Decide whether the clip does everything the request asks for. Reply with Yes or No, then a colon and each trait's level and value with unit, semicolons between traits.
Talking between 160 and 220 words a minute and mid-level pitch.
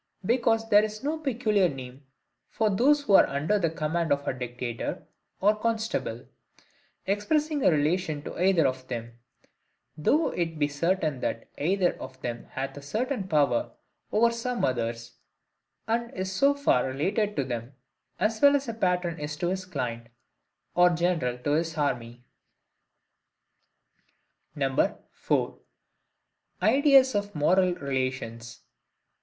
No: average, 140 wpm; medium, 175 Hz